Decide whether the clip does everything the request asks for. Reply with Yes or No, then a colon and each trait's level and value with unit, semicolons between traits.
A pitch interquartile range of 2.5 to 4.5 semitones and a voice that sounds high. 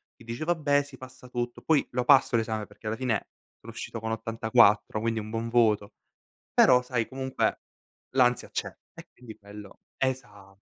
No: average, 2.8 semitones; low, 115 Hz